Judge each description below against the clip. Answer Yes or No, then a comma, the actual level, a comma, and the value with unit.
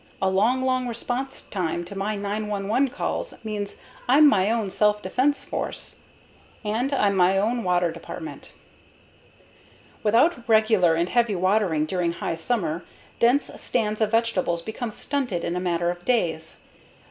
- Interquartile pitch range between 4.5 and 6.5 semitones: Yes, average, 4.8 semitones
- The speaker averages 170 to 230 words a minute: No, average, 145 wpm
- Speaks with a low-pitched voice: No, high, 210 Hz